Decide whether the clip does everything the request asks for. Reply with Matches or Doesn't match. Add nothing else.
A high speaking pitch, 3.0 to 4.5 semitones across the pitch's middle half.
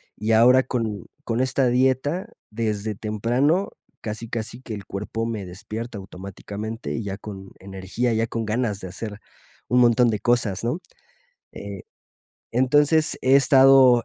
Doesn't match